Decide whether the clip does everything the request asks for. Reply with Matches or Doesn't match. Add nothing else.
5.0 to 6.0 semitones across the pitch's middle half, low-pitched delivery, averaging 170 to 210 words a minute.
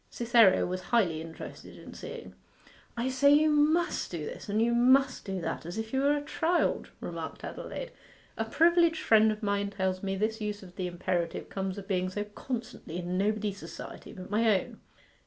Doesn't match